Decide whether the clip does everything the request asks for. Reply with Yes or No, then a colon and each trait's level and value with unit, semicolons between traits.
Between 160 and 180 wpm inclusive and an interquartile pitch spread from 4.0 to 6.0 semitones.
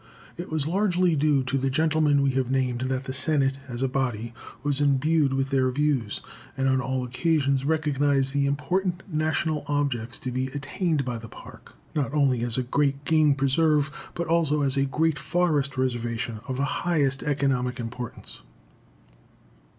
No: average, 165 wpm; average, 2.7 semitones